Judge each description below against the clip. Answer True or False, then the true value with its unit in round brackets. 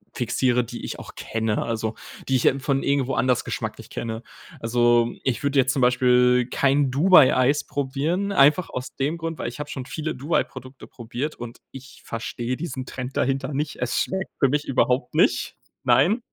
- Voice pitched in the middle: False (130 Hz)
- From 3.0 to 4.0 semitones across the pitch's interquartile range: False (2.6 semitones)